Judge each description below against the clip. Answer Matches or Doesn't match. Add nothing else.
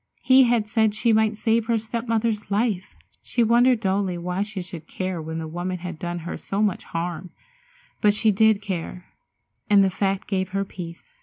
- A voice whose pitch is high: Matches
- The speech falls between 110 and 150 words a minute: Doesn't match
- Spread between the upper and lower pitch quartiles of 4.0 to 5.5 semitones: Doesn't match